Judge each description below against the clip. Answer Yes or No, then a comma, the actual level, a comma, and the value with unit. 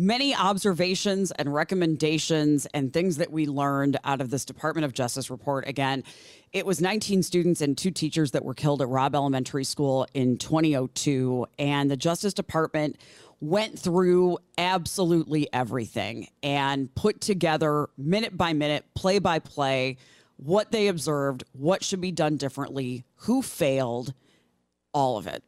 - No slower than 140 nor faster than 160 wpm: Yes, average, 150 wpm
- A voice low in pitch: No, medium, 150 Hz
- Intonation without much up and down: No, average, 4.8 semitones